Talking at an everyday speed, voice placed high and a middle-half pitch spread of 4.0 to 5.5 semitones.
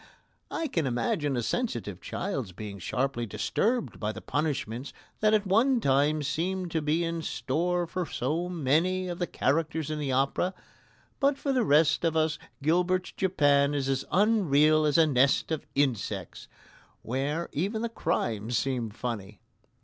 No: average, 155 wpm; medium, 155 Hz; average, 5.2 semitones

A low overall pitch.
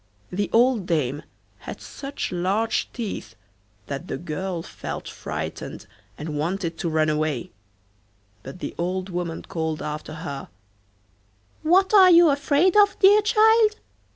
No: medium, 185 Hz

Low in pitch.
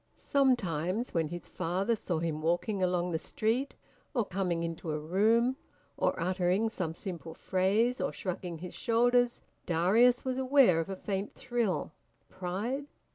No: high, 190 Hz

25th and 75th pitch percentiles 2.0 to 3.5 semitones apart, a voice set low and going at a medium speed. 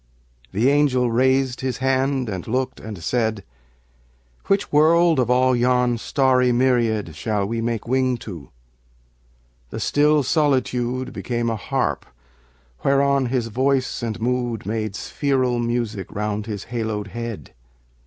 No: average, 2.9 semitones; low, 125 Hz; slow, 130 wpm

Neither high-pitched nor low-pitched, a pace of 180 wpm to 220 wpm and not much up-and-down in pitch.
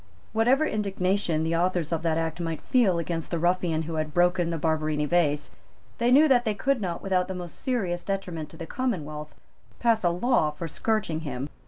No: medium, 175 Hz; average, 195 wpm; average, 4.3 semitones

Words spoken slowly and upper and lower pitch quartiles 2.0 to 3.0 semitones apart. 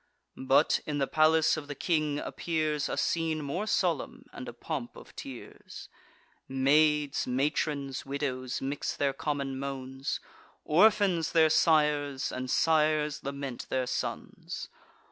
Yes: slow, 125 wpm; narrow, 2.5 semitones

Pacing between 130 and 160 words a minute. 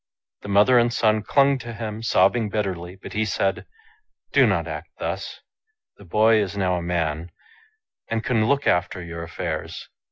No: average, 170 wpm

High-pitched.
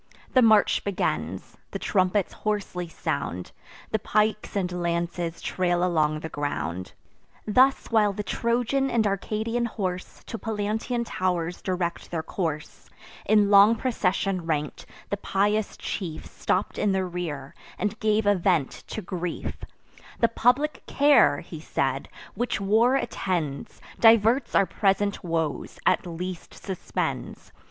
Yes: high, 195 Hz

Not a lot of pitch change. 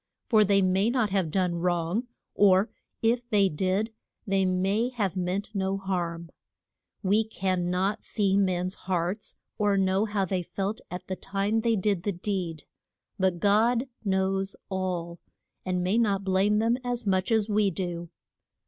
Yes: narrow, 2.3 semitones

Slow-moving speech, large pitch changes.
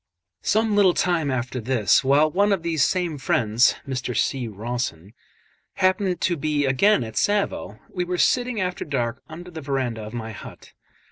No: average, 165 wpm; wide, 6.9 semitones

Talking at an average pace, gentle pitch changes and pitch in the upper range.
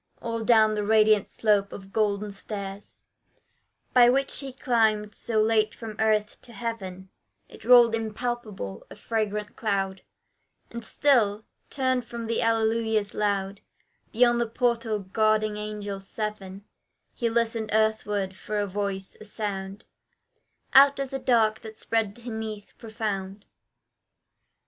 No: slow, 130 wpm; narrow, 2.1 semitones; high, 215 Hz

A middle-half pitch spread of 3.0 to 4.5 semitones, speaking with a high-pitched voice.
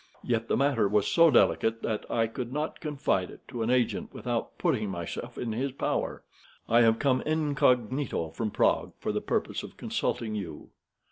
No: average, 4.0 semitones; low, 115 Hz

